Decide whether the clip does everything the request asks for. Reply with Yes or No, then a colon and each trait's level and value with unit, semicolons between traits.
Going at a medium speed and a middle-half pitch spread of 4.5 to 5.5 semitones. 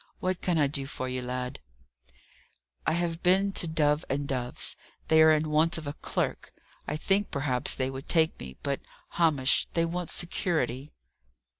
No: average, 170 wpm; average, 3.9 semitones